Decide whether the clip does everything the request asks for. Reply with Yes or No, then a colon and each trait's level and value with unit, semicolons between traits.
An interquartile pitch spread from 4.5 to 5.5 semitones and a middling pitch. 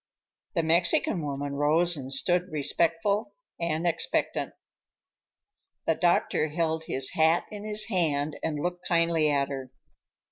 No: average, 3.0 semitones; medium, 165 Hz